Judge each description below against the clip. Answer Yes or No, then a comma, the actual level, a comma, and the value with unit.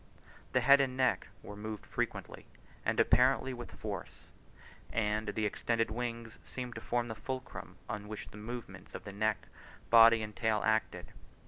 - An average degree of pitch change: No, narrow, 2.3 semitones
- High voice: No, low, 115 Hz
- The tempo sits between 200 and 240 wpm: No, average, 160 wpm